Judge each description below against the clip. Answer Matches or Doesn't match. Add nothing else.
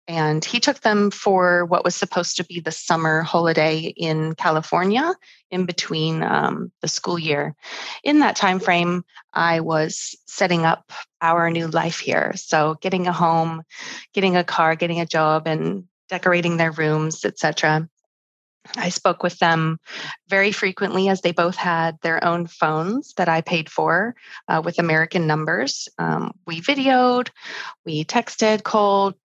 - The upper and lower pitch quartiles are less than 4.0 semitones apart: Matches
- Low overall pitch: Doesn't match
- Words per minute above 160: Doesn't match